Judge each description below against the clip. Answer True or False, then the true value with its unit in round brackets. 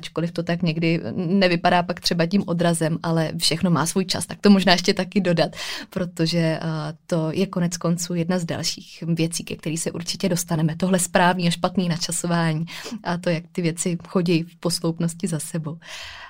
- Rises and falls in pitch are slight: True (1.8 semitones)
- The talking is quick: True (180 wpm)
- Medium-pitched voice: True (170 Hz)